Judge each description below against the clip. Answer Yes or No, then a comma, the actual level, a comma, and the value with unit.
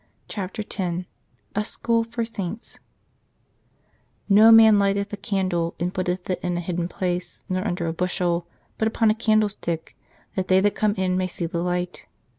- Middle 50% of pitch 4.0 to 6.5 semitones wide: No, average, 3.0 semitones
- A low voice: No, medium, 185 Hz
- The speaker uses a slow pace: No, average, 175 wpm